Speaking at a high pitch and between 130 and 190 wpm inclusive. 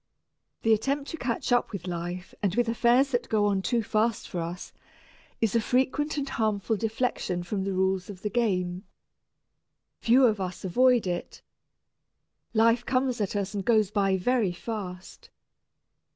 Yes: high, 215 Hz; average, 160 wpm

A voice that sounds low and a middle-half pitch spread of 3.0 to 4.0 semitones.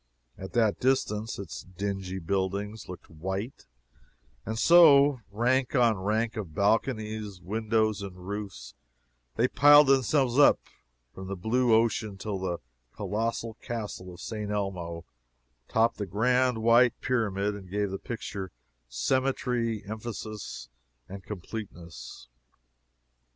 Yes: low, 105 Hz; average, 3.4 semitones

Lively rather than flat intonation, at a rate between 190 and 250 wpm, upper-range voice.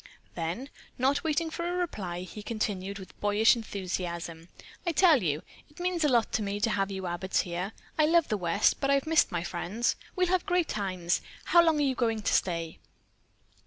Yes: wide, 8.8 semitones; average, 200 wpm; high, 215 Hz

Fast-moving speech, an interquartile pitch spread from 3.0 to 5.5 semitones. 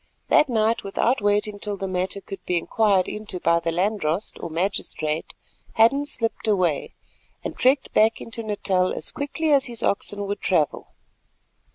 No: average, 160 wpm; average, 3.6 semitones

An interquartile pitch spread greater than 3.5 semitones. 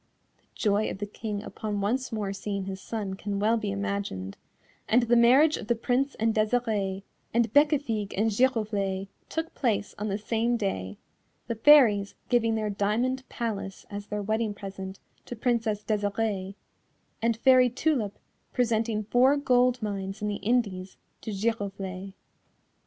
No: average, 3.0 semitones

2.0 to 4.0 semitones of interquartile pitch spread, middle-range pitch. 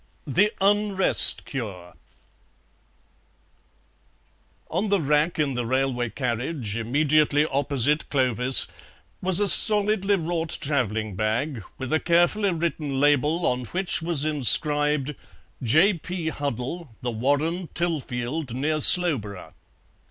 No: wide, 5.4 semitones; medium, 145 Hz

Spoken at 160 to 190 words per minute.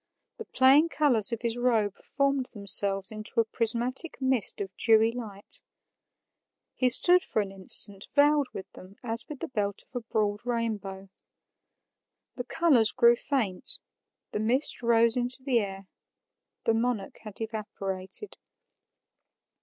No: average, 140 wpm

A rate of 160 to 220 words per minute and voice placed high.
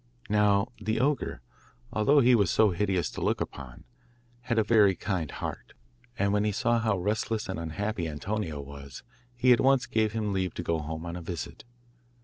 No: average, 185 wpm; low, 105 Hz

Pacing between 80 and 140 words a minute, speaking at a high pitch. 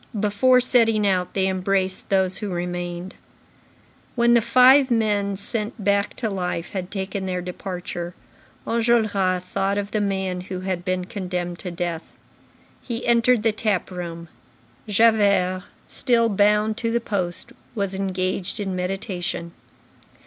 Yes: slow, 135 wpm; high, 195 Hz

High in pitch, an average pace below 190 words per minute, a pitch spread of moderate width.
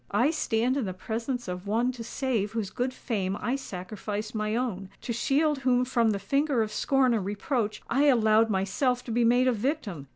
No: high, 230 Hz; average, 195 wpm; average, 3.6 semitones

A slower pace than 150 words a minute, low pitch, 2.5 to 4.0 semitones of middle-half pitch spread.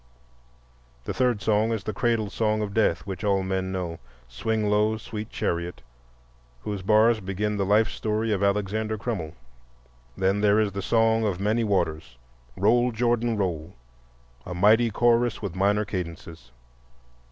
Yes: average, 140 wpm; low, 105 Hz; average, 3.4 semitones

